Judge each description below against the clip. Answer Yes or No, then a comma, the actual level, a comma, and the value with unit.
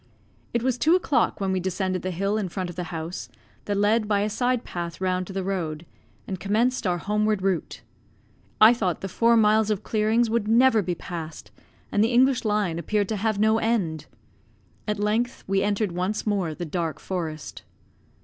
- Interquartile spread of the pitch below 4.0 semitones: Yes, average, 3.3 semitones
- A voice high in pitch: Yes, high, 205 Hz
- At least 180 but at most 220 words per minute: Yes, average, 190 wpm